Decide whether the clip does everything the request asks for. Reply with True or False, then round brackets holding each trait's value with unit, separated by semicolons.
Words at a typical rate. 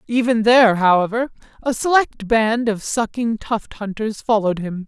True (150 wpm)